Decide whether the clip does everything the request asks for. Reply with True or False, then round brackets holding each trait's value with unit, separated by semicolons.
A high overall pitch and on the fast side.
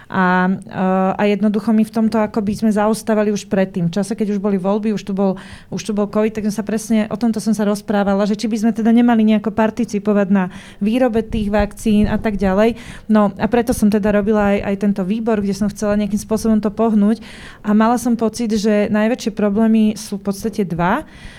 True (215 Hz; 215 wpm)